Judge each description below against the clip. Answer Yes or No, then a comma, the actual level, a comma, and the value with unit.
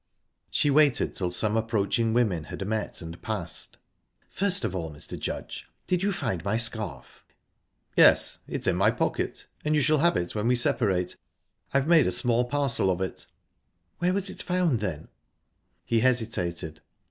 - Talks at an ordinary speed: Yes, average, 165 wpm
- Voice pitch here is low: Yes, low, 115 Hz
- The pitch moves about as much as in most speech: No, wide, 7.4 semitones